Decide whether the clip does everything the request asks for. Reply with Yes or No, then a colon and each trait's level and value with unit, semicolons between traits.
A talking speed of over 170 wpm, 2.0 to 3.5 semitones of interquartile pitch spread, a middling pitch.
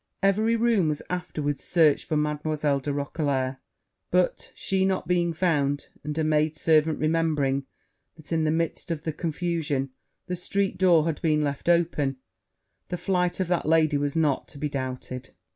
No: average, 165 wpm; average, 3.1 semitones; medium, 155 Hz